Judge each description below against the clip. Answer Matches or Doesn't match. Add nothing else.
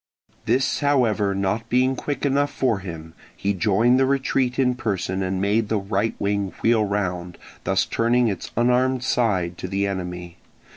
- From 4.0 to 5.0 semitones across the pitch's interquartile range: Matches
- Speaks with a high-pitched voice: Doesn't match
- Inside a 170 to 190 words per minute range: Doesn't match